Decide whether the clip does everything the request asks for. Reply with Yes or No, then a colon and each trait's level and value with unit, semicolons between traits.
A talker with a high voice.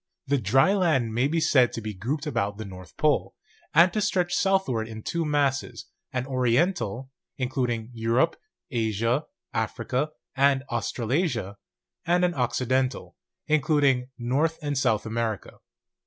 No: low, 130 Hz